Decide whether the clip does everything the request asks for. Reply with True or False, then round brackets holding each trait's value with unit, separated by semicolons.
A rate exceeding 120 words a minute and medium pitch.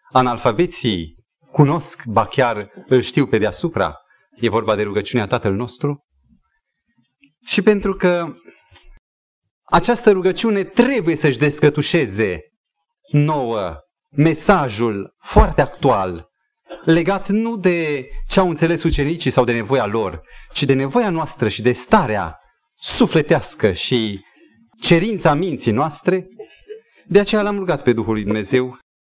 False (115 wpm; 145 Hz)